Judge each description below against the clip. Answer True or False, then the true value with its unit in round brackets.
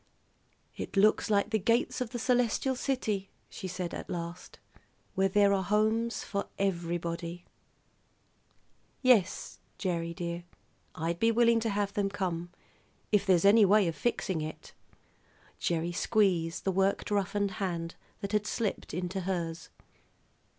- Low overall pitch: False (195 Hz)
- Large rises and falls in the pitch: False (3.7 semitones)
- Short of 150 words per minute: True (135 wpm)